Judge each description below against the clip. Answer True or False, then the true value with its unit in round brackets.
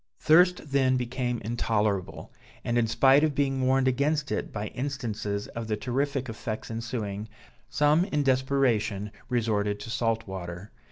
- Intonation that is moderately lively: True (4.1 semitones)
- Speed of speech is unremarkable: True (145 wpm)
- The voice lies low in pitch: True (120 Hz)